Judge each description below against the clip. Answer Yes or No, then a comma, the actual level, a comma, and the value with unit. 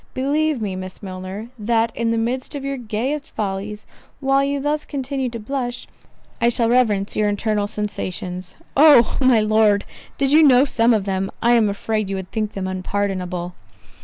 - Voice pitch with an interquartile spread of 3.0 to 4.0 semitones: No, average, 4.5 semitones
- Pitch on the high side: Yes, high, 225 Hz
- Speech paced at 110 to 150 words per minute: No, average, 175 wpm